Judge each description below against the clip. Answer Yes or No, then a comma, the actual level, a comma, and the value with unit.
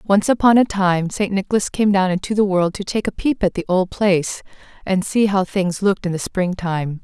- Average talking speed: No, fast, 240 wpm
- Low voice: No, high, 190 Hz